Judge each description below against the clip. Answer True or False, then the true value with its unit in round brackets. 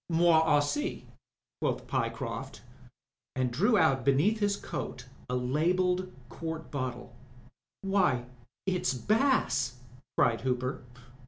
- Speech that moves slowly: True (105 wpm)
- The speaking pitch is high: False (150 Hz)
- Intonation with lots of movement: True (6.3 semitones)